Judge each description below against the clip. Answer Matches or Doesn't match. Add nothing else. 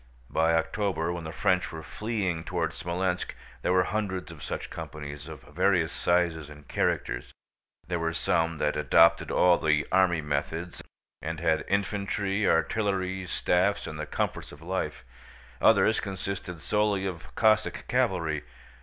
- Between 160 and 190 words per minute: Doesn't match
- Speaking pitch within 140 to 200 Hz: Doesn't match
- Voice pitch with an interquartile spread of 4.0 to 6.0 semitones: Doesn't match